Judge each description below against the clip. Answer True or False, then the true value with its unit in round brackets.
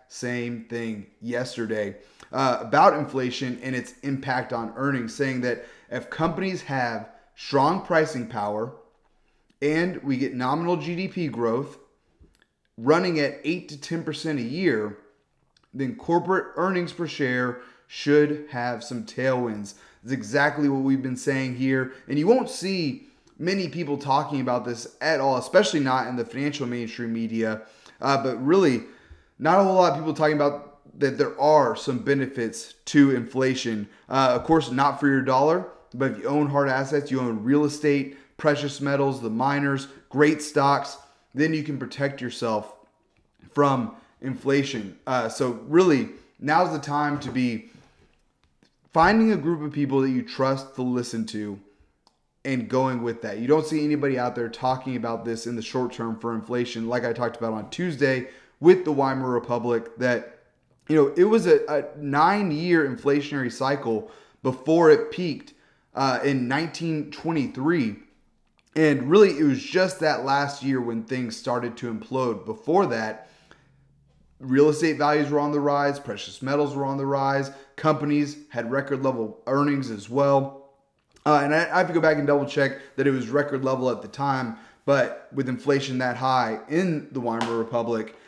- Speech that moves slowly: False (160 wpm)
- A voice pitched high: False (135 Hz)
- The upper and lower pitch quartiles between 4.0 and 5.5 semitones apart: False (3.2 semitones)